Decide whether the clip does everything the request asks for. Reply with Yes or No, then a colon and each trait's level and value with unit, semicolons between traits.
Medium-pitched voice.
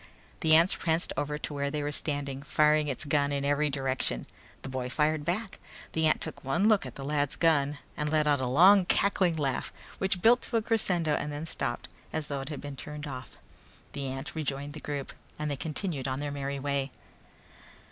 Yes: medium, 145 Hz